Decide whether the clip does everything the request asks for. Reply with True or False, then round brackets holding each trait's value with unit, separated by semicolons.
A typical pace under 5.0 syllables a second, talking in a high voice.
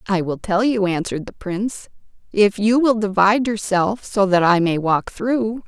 True (4.7 syllables/s; 205 Hz)